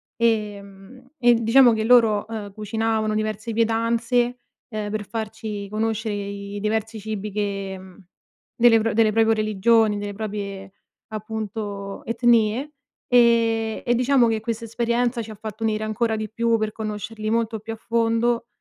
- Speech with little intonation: Yes, narrow, 1.6 semitones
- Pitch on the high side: Yes, high, 220 Hz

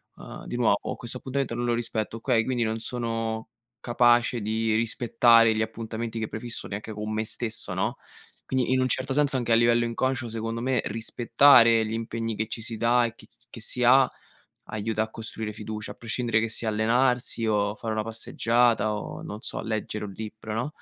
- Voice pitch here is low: Yes, low, 115 Hz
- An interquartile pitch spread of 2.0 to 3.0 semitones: No, narrow, 1.6 semitones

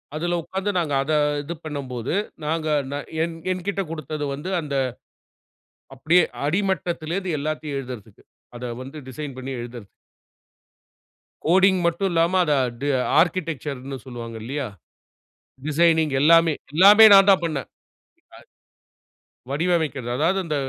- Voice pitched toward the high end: No, medium, 155 Hz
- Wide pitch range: No, average, 4.0 semitones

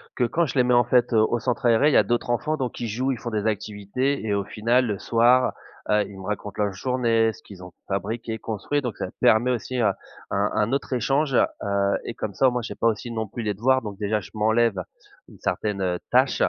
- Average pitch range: Yes, average, 3.0 semitones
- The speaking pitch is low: Yes, low, 115 Hz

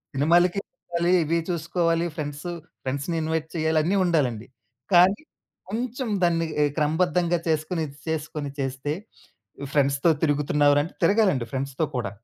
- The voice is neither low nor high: Yes, medium, 160 Hz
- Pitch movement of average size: Yes, average, 3.2 semitones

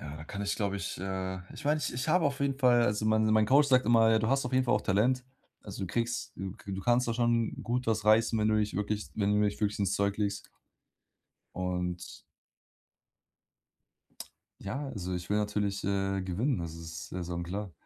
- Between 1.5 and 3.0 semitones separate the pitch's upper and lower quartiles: No, average, 3.7 semitones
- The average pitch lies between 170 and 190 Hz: No, low, 105 Hz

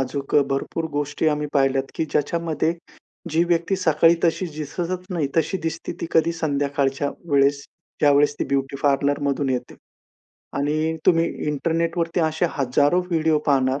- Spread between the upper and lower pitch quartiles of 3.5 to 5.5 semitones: No, average, 2.9 semitones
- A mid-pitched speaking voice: Yes, medium, 150 Hz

